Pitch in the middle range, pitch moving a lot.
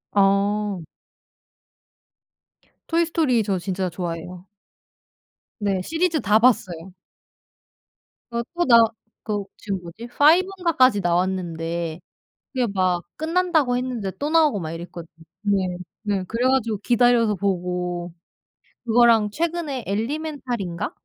No: high, 210 Hz; wide, 5.9 semitones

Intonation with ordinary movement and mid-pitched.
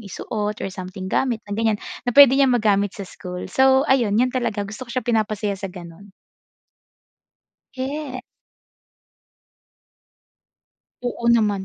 No: average, 4.0 semitones; high, 215 Hz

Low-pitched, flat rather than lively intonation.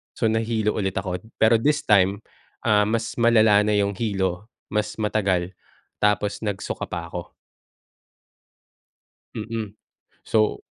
Yes: low, 105 Hz; narrow, 2.2 semitones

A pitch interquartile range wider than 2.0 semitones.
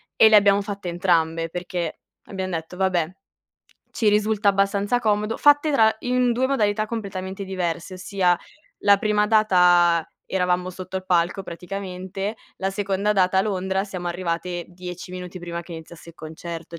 Yes: average, 2.7 semitones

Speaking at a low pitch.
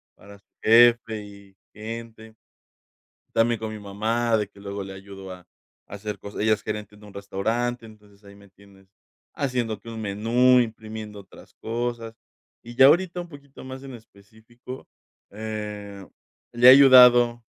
Yes: low, 110 Hz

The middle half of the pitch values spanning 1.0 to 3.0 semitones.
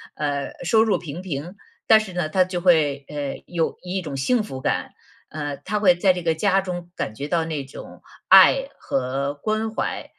No: average, 4.8 semitones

